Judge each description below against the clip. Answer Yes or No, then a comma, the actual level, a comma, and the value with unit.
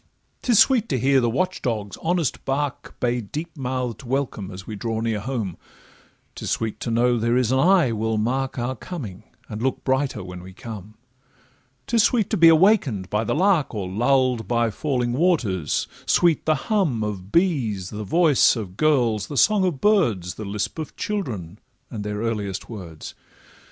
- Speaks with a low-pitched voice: Yes, low, 120 Hz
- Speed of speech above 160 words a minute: Yes, average, 175 wpm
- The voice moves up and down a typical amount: No, wide, 6.5 semitones